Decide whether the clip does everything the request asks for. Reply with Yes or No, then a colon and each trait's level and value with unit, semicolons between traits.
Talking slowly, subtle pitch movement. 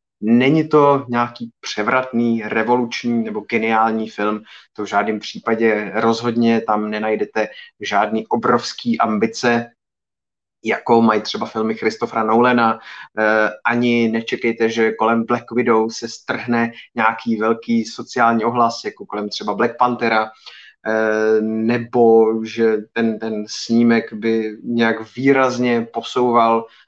Yes: slow, 110 wpm; narrow, 1.3 semitones